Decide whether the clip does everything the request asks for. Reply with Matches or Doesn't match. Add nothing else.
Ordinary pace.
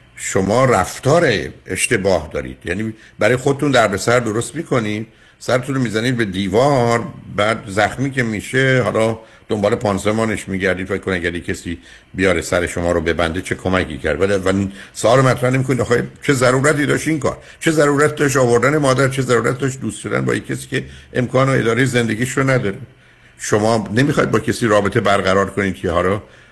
Doesn't match